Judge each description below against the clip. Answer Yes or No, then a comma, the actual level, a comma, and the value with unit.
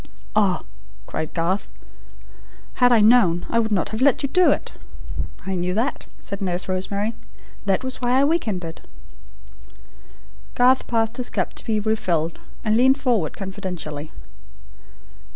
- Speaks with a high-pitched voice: Yes, high, 215 Hz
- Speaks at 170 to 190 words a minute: No, average, 145 wpm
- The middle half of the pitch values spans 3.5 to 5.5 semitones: Yes, average, 5.1 semitones